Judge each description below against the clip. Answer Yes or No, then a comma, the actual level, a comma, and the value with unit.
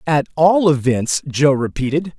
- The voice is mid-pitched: Yes, medium, 150 Hz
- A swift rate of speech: No, slow, 135 wpm